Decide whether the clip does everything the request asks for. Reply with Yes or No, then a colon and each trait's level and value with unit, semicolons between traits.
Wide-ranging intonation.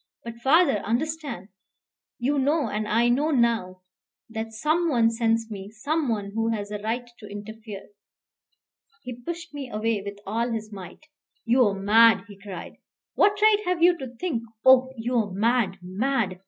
No: average, 4.2 semitones